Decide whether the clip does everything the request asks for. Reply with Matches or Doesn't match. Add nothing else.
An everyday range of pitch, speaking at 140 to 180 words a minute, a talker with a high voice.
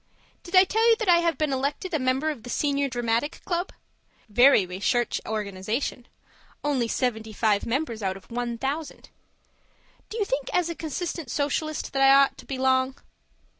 Matches